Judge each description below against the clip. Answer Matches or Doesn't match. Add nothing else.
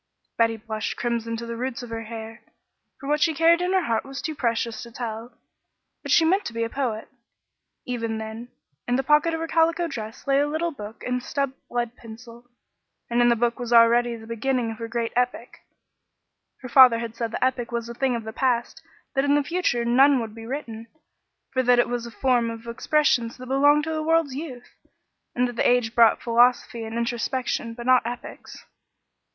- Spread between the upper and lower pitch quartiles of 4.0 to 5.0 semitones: Doesn't match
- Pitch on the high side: Matches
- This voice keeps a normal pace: Doesn't match